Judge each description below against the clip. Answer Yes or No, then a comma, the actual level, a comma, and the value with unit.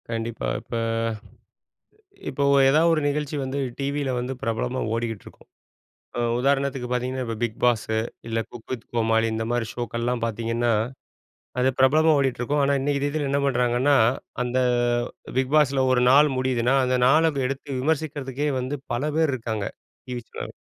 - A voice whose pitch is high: No, low, 130 Hz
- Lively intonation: No, average, 3.0 semitones